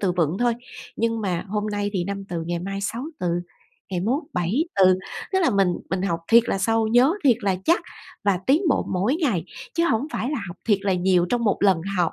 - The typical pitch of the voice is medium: No, high, 200 Hz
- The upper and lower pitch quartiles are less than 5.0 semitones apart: Yes, average, 4.3 semitones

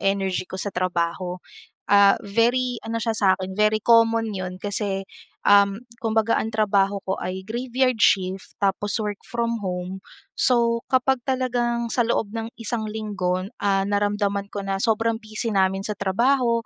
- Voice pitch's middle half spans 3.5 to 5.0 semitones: No, average, 3.1 semitones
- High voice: Yes, high, 205 Hz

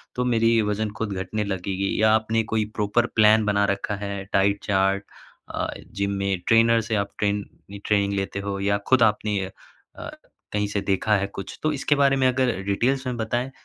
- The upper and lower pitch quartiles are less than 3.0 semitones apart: Yes, narrow, 2.4 semitones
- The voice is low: Yes, low, 105 Hz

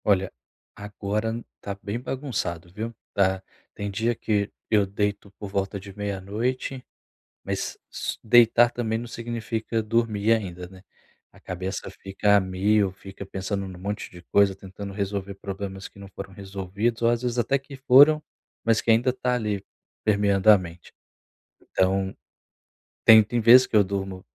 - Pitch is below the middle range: Yes, low, 100 Hz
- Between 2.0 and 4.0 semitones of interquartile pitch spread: Yes, average, 2.9 semitones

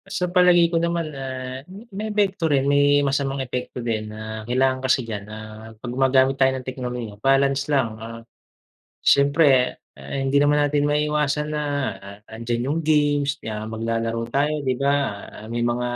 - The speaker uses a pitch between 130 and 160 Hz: Yes, low, 135 Hz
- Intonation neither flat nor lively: Yes, average, 3.8 semitones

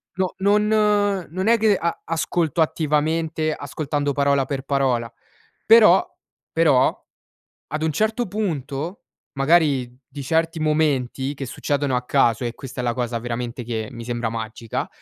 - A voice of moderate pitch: Yes, medium, 145 Hz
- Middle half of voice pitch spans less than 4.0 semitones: No, average, 5.2 semitones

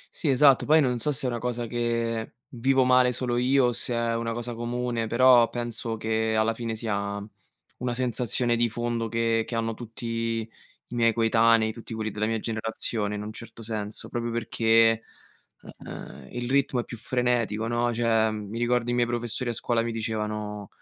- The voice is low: Yes, low, 115 Hz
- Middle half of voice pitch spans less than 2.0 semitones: Yes, narrow, 1.3 semitones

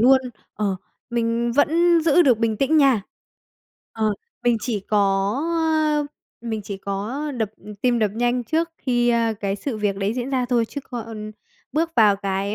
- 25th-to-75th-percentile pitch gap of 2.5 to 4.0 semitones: Yes, average, 3.6 semitones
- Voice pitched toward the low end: No, high, 235 Hz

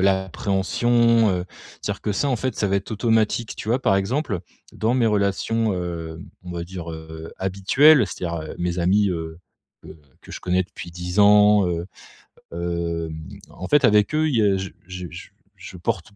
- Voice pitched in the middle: No, very low, 95 Hz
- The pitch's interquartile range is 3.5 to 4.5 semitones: Yes, average, 4.0 semitones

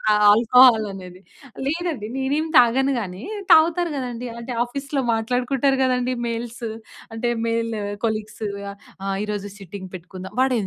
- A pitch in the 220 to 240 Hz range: Yes, high, 235 Hz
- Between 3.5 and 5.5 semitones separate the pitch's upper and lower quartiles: Yes, average, 4.0 semitones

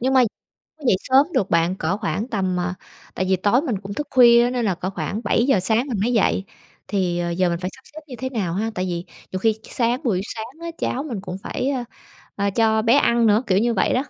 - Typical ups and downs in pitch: Yes, average, 4.7 semitones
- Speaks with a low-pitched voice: No, high, 220 Hz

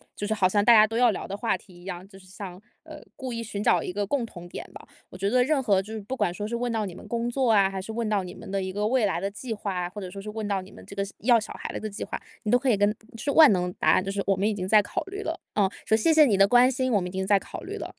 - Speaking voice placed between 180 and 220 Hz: Yes, high, 210 Hz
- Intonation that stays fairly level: No, average, 3.4 semitones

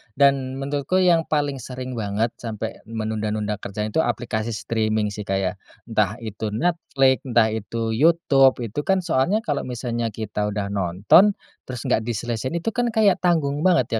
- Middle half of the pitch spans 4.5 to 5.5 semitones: Yes, average, 4.9 semitones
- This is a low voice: Yes, low, 120 Hz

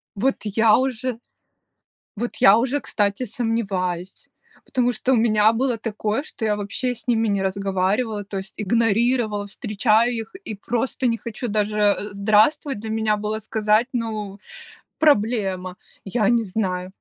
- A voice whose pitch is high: Yes, high, 215 Hz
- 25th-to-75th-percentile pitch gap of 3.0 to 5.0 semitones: No, narrow, 2.6 semitones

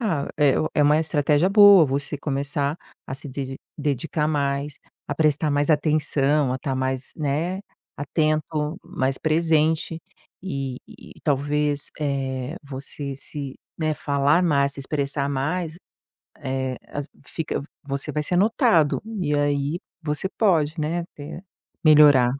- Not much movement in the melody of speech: Yes, narrow, 2.1 semitones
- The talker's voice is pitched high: No, medium, 145 Hz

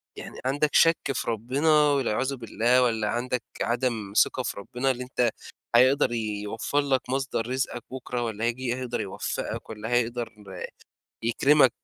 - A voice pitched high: No, low, 125 Hz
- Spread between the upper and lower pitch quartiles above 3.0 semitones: No, narrow, 2.4 semitones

